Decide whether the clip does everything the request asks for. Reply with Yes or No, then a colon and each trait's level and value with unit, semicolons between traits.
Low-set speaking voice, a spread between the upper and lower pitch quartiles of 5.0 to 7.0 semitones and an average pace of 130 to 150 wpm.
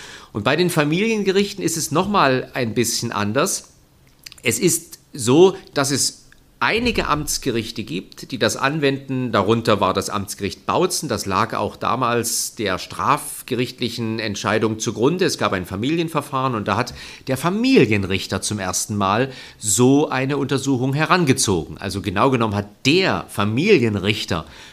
Yes: low, 120 Hz; average, 5.3 semitones; average, 140 wpm